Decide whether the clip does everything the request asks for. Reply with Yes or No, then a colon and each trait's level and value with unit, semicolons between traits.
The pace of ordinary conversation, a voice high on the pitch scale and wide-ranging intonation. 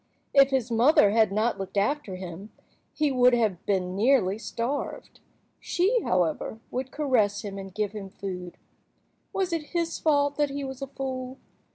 Yes: average, 165 wpm; high, 240 Hz; wide, 5.9 semitones